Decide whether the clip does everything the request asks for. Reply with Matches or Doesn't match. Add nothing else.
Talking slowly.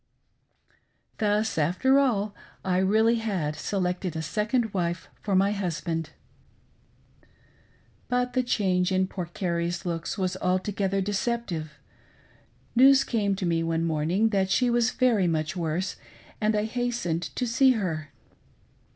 Matches